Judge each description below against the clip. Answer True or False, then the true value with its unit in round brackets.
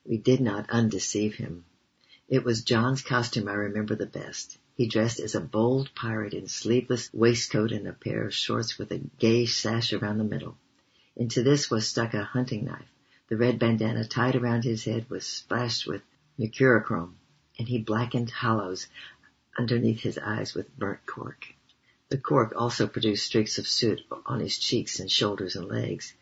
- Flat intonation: True (2.2 semitones)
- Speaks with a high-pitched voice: False (115 Hz)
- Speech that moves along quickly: False (175 wpm)